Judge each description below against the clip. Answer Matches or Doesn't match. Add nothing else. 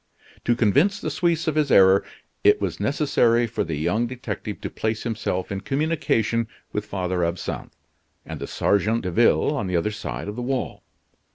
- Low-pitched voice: Matches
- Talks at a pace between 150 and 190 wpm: Matches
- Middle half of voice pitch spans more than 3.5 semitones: Matches